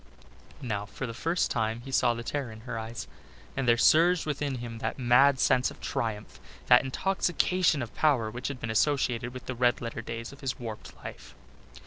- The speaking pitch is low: Yes, low, 125 Hz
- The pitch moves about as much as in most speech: Yes, average, 3.3 semitones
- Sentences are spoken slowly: No, average, 195 wpm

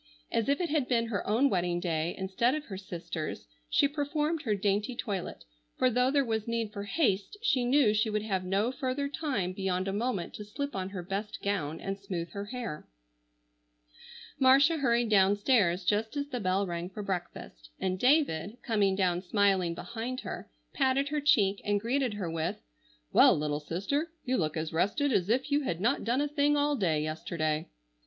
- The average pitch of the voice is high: Yes, high, 210 Hz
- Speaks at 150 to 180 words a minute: No, average, 190 wpm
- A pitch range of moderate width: No, wide, 5.9 semitones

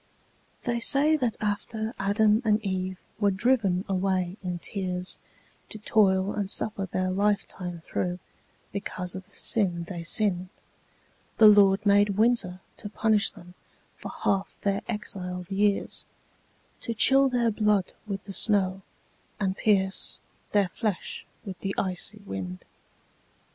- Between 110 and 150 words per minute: Yes, slow, 135 wpm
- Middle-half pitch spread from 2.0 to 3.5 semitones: Yes, narrow, 2.4 semitones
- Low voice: No, high, 200 Hz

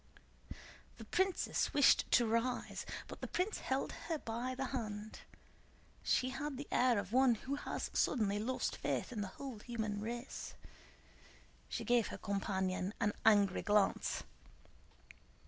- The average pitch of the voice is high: Yes, high, 235 Hz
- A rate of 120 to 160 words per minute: Yes, average, 140 wpm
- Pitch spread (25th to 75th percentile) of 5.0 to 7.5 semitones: No, average, 3.9 semitones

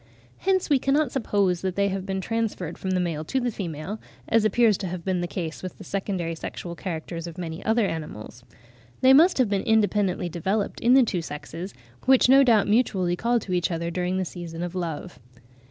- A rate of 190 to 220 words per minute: Yes, fast, 205 wpm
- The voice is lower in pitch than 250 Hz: Yes, high, 190 Hz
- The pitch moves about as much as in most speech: Yes, average, 4.5 semitones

